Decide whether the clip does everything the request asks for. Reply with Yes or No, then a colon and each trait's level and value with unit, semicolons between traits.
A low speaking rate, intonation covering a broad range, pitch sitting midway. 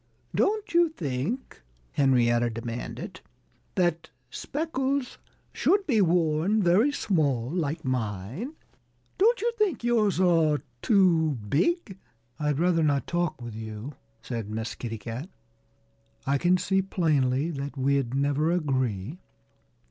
Yes: slow, 120 wpm; wide, 7.2 semitones; medium, 155 Hz